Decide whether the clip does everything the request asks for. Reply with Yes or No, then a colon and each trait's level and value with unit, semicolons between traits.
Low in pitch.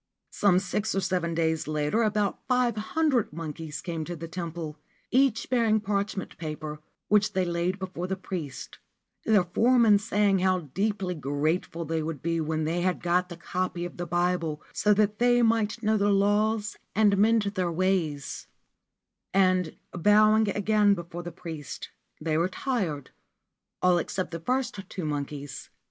No: medium, 185 Hz